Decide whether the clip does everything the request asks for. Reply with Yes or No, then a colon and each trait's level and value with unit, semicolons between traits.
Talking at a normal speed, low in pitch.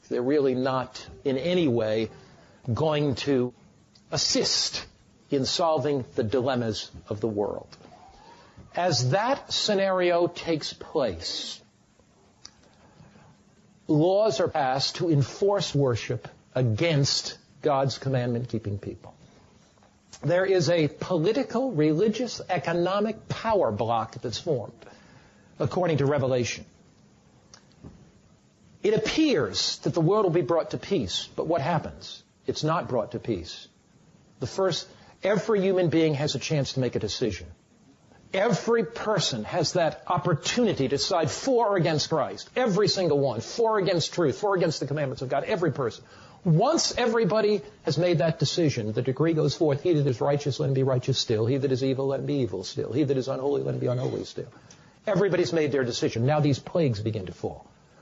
No: average, 155 wpm; medium, 150 Hz